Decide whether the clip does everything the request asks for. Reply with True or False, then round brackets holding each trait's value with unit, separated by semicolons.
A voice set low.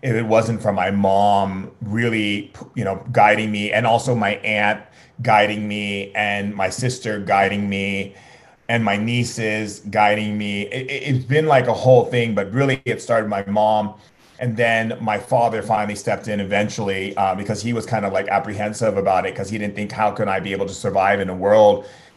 True (105 Hz)